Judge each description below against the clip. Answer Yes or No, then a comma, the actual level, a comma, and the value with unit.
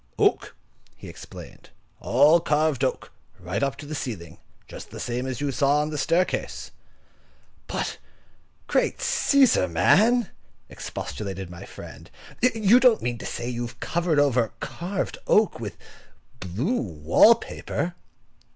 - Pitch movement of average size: No, wide, 8.2 semitones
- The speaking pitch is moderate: Yes, medium, 145 Hz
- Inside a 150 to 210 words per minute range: No, slow, 135 wpm